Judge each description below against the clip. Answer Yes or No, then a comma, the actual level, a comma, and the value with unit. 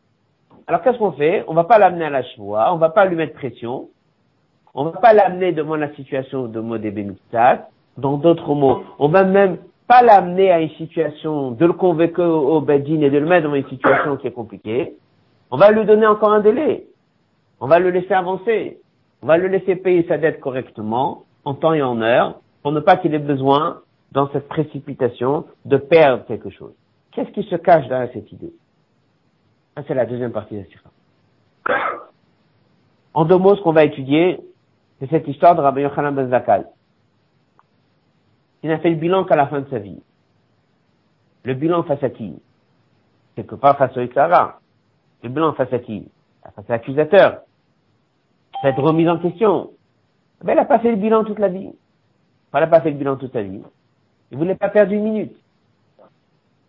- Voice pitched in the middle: Yes, medium, 155 Hz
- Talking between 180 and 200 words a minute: Yes, average, 195 wpm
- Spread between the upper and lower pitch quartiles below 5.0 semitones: No, average, 5.3 semitones